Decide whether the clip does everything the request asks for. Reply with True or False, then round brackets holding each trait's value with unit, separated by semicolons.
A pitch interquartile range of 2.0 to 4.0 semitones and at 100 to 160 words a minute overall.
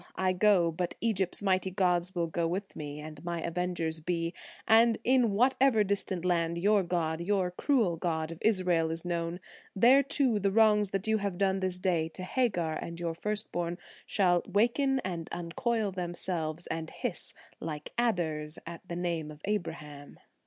False (3.7 semitones; 170 wpm)